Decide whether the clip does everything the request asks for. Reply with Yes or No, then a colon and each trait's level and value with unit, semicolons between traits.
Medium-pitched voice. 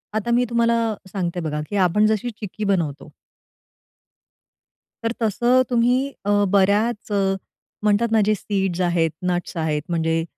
No: high, 205 Hz